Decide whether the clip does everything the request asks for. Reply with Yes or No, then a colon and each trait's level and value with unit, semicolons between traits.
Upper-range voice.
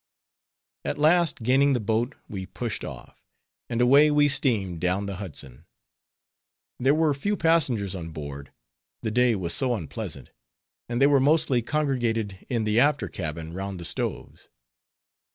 No: low, 115 Hz